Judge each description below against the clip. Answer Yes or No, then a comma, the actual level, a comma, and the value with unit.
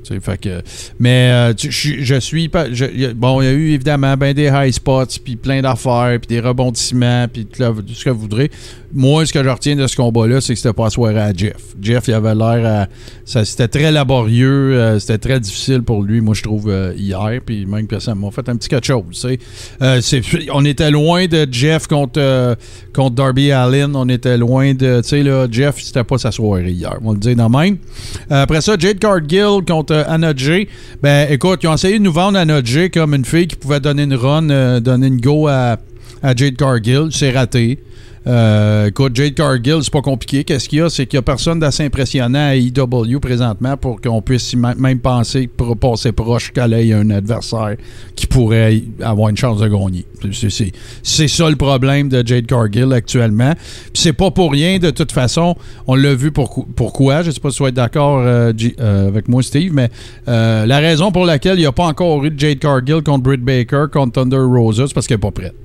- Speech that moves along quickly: Yes, fast, 225 wpm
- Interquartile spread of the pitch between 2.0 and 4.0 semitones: Yes, average, 3.7 semitones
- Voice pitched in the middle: No, low, 130 Hz